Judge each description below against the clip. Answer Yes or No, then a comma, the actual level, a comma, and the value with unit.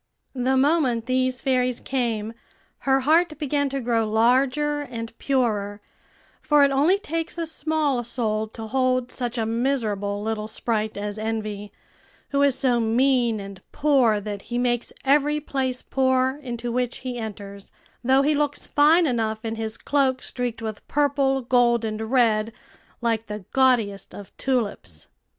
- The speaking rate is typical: Yes, average, 150 wpm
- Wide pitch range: No, average, 3.6 semitones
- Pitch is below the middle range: No, high, 245 Hz